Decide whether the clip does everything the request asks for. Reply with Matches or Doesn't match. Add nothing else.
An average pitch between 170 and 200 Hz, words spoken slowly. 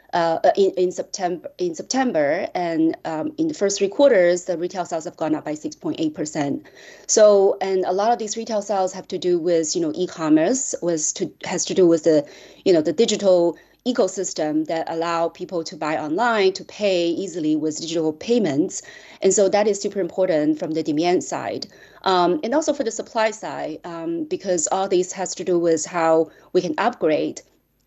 Doesn't match